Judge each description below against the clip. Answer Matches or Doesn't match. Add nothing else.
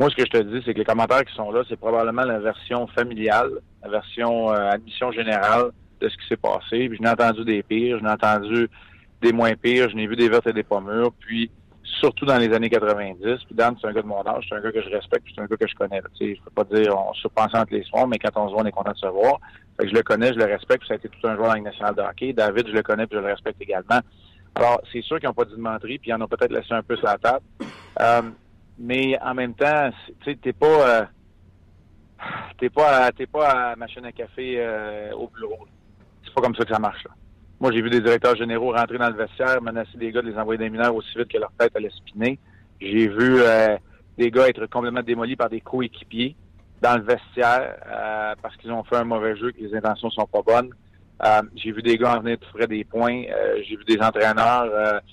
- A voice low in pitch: Matches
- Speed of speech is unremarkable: Doesn't match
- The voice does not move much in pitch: Matches